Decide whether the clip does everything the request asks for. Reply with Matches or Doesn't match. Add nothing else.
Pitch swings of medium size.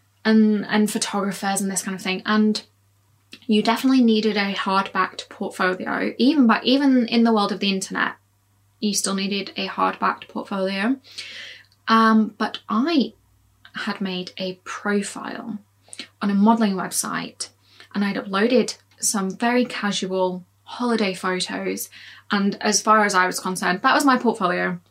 Matches